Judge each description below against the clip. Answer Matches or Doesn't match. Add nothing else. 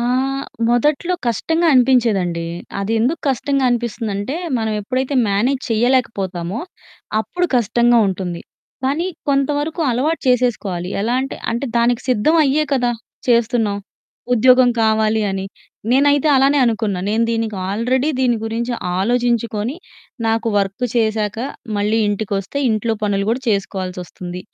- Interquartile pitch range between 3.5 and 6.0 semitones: Matches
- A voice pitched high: Matches